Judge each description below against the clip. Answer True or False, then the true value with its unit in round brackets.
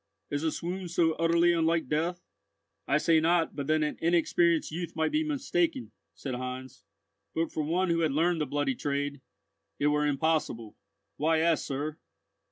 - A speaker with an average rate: True (170 wpm)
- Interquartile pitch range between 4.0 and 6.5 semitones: False (2.6 semitones)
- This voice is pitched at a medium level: True (160 Hz)